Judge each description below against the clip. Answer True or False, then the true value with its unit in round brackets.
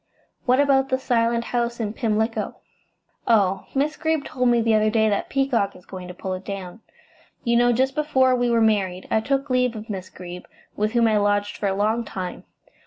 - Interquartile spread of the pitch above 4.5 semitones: False (3.7 semitones)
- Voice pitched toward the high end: True (225 Hz)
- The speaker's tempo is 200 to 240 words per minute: True (205 wpm)